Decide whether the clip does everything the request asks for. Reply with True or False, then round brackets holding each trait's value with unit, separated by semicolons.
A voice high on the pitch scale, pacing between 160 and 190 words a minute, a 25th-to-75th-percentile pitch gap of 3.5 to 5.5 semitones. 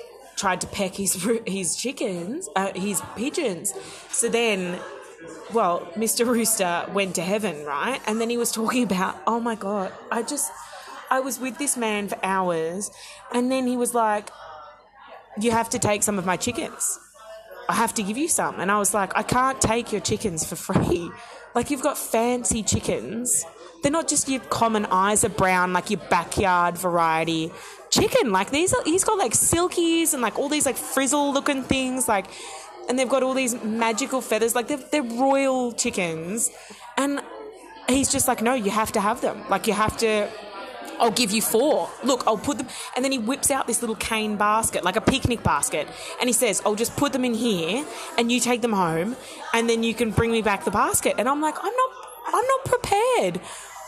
False (230 Hz; 200 wpm; 4.3 semitones)